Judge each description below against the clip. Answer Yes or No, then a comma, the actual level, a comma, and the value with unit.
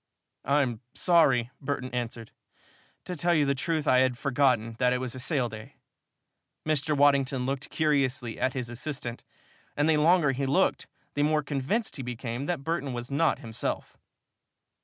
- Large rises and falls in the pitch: No, average, 3.2 semitones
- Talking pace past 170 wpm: No, average, 160 wpm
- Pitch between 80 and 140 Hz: Yes, low, 135 Hz